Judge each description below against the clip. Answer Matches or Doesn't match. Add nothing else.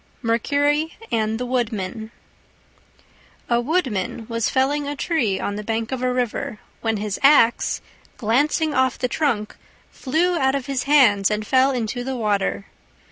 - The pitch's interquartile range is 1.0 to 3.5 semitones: Doesn't match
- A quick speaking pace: Doesn't match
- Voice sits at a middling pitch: Doesn't match